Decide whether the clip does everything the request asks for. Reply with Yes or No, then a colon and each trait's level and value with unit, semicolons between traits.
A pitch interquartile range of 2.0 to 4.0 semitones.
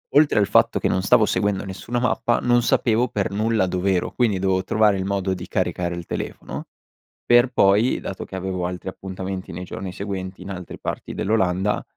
Yes: narrow, 2.6 semitones